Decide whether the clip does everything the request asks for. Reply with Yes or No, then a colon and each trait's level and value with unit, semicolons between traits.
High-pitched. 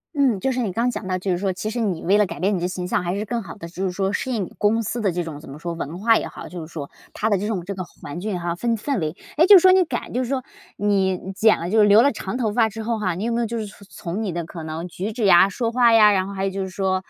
Yes: high, 200 Hz